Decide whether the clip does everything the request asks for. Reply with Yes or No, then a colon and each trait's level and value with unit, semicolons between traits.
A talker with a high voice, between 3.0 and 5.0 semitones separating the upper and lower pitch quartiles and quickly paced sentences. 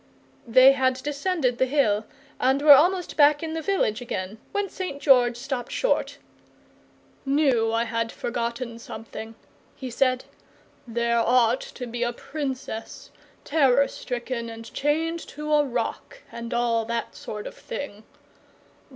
No: very high, 255 Hz; average, 3.7 semitones; average, 140 wpm